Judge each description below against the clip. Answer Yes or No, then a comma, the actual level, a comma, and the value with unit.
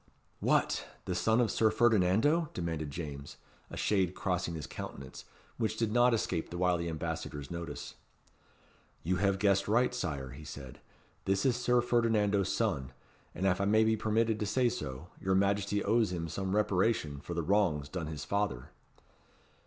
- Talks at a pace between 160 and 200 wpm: Yes, average, 165 wpm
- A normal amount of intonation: Yes, average, 5.0 semitones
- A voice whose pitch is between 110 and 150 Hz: No, very low, 95 Hz